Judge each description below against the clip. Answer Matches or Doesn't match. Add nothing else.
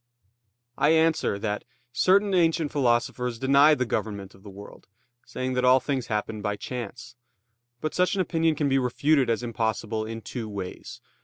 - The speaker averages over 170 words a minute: Doesn't match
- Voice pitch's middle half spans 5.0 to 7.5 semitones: Matches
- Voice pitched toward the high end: Doesn't match